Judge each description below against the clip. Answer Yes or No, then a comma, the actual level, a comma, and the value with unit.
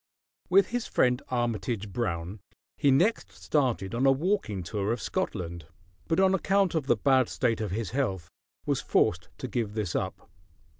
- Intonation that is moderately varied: No, wide, 6.3 semitones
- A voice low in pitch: Yes, low, 120 Hz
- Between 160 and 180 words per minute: Yes, average, 165 wpm